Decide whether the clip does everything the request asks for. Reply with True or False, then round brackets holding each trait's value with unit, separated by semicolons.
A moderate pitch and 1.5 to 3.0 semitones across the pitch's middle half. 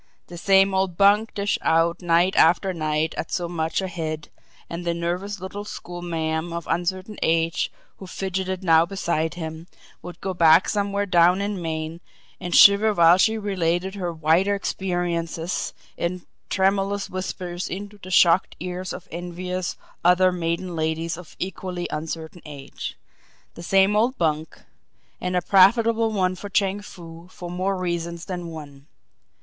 True (180 Hz; 2.4 semitones)